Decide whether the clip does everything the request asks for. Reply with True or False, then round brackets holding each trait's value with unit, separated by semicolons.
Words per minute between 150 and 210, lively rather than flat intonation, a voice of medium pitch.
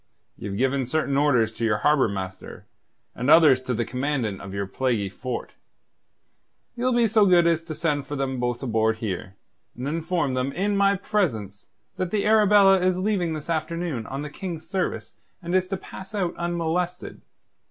True (175 wpm; 6.8 semitones; 150 Hz)